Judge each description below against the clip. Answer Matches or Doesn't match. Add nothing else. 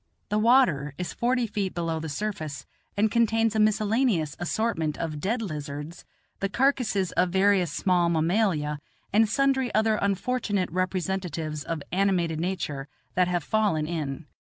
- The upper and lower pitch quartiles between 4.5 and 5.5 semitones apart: Matches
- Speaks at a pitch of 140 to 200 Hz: Matches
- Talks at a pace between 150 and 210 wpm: Doesn't match